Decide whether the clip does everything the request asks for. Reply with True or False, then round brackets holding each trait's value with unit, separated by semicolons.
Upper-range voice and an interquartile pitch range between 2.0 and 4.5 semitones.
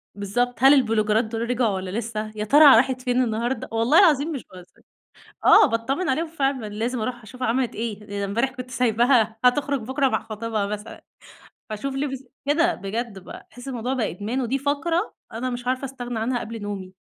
True (245 Hz; 3.4 semitones)